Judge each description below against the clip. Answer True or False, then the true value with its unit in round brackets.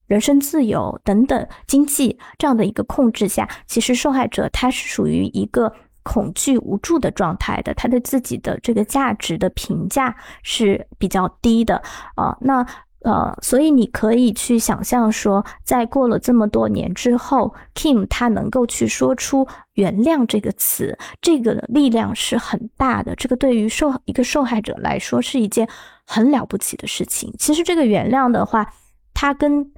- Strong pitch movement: False (3.7 semitones)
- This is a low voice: False (240 Hz)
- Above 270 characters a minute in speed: False (260 characters per minute)